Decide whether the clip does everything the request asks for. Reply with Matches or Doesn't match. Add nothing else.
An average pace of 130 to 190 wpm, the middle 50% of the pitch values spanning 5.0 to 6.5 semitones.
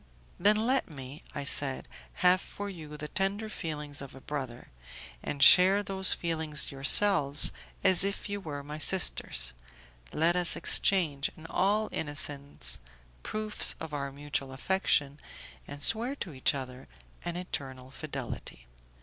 Matches